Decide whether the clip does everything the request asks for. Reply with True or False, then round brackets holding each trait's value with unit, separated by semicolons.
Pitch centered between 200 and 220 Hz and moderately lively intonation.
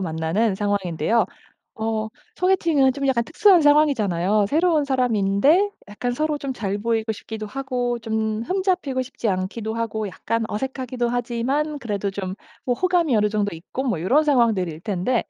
False (230 Hz; 5.0 semitones)